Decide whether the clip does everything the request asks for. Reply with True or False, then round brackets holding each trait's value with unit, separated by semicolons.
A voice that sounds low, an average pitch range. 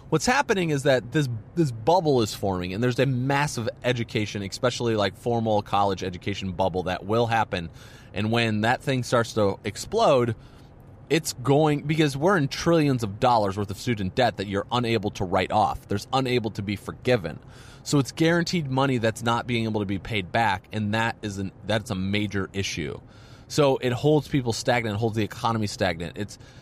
True (115 Hz; 4.0 semitones)